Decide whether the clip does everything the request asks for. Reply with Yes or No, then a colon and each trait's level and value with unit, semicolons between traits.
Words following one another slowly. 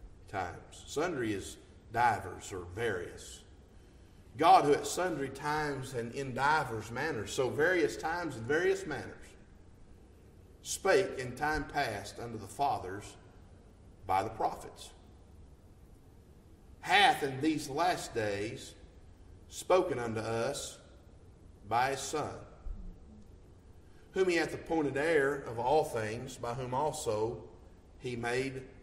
Yes: slow, 115 wpm